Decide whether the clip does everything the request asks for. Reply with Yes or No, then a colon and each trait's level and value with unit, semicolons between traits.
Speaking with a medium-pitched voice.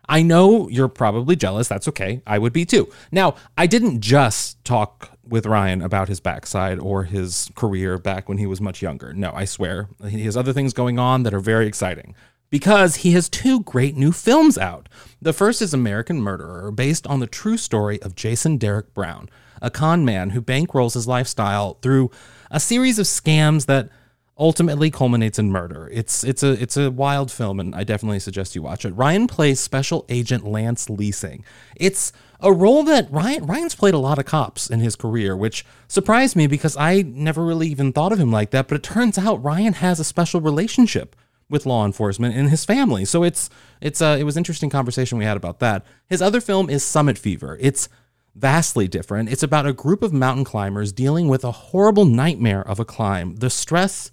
No: low, 130 Hz